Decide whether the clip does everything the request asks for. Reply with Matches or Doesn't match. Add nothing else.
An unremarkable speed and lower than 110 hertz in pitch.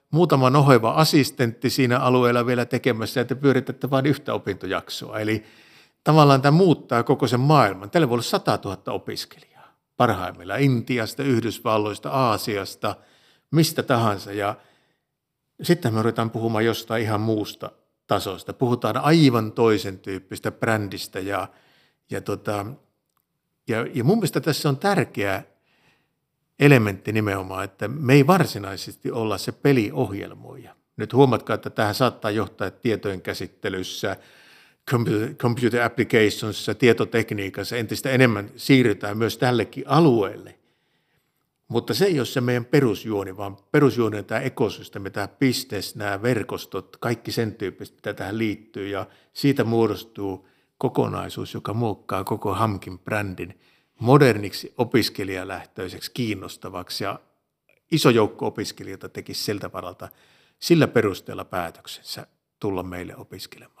Doesn't match